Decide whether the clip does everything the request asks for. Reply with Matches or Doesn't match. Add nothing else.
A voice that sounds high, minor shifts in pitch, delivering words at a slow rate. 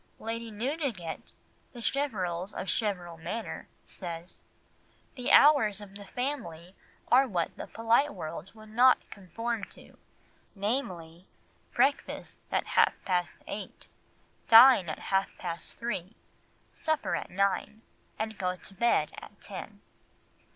Doesn't match